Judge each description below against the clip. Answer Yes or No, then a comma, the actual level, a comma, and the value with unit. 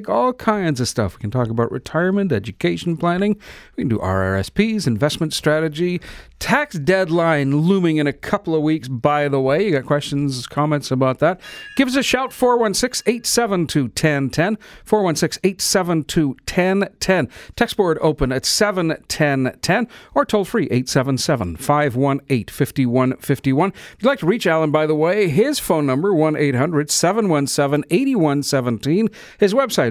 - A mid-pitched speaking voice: Yes, medium, 155 Hz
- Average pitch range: No, wide, 6.2 semitones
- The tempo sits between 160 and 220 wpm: No, average, 145 wpm